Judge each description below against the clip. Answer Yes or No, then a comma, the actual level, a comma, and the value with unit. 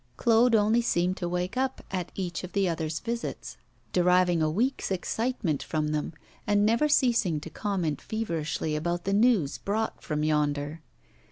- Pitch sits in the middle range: Yes, medium, 180 Hz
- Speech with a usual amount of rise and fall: No, wide, 6.0 semitones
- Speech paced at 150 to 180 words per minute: Yes, average, 160 wpm